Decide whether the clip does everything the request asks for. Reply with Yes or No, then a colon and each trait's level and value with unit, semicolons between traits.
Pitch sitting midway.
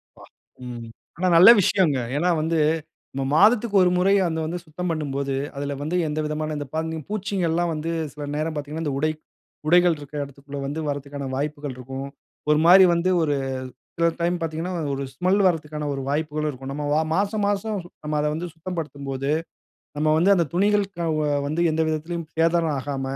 Yes: medium, 155 Hz